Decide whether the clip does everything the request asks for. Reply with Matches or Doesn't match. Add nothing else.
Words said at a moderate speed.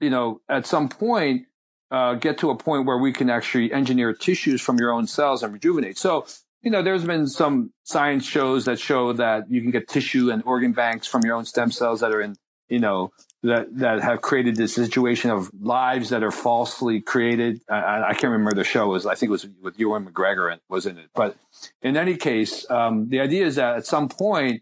Doesn't match